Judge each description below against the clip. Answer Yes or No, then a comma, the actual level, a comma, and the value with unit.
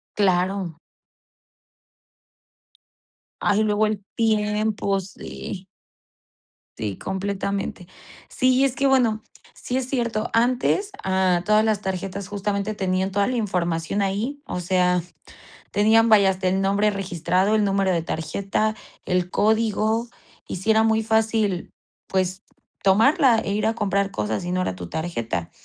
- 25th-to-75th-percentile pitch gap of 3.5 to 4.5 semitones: No, average, 2.9 semitones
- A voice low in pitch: No, high, 200 Hz